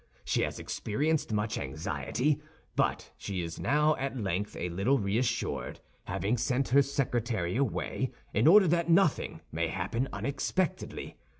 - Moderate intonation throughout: No, wide, 6.2 semitones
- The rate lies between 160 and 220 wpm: No, slow, 135 wpm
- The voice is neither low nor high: No, low, 120 Hz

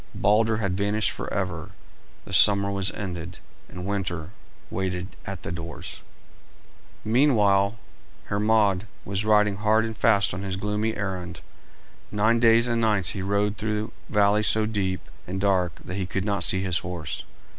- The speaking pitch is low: Yes, low, 100 Hz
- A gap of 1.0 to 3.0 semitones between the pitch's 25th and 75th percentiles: Yes, narrow, 2.4 semitones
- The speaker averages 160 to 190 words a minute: No, average, 150 wpm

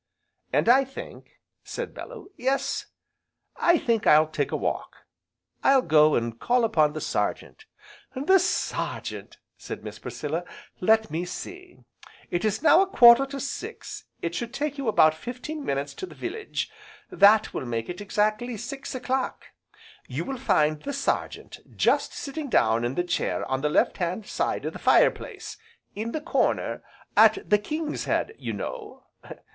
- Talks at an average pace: Yes, average, 160 wpm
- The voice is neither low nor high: No, high, 235 Hz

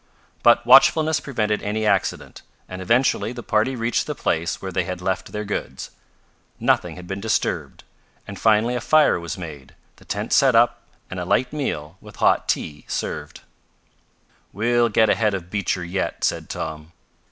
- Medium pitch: No, low, 105 Hz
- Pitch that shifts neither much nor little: Yes, average, 4.9 semitones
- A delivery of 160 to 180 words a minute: Yes, average, 165 wpm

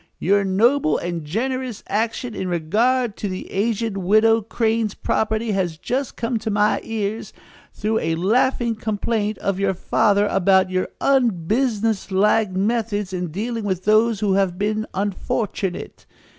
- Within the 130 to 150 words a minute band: Yes, average, 140 wpm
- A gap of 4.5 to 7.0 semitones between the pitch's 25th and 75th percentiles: No, average, 2.9 semitones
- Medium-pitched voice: No, high, 210 Hz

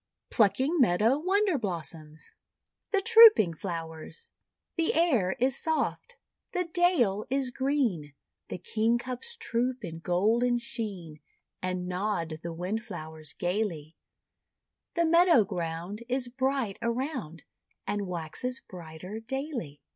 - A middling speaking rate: No, slow, 110 wpm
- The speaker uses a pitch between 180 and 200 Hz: No, high, 220 Hz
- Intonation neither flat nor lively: No, wide, 7.5 semitones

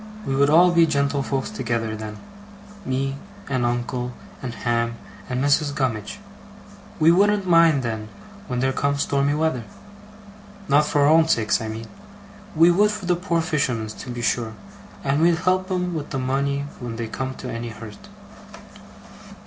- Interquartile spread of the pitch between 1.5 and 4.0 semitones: No, average, 5.2 semitones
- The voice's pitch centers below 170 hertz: Yes, medium, 140 Hz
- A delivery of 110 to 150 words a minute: No, average, 160 wpm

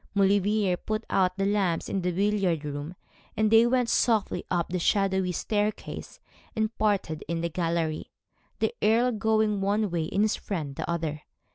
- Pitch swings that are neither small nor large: Yes, average, 4.0 semitones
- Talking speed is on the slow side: No, average, 170 wpm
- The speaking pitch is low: No, high, 195 Hz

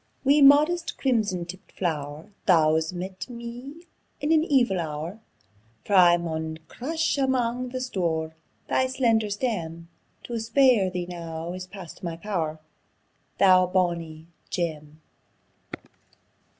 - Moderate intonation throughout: No, wide, 6.9 semitones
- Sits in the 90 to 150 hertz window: No, medium, 185 Hz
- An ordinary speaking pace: No, slow, 120 wpm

